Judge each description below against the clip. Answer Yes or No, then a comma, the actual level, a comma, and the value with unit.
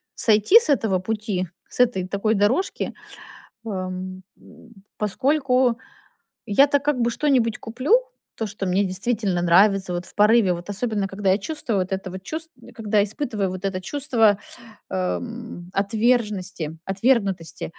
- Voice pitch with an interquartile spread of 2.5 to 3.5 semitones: No, average, 4.1 semitones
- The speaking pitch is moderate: No, high, 210 Hz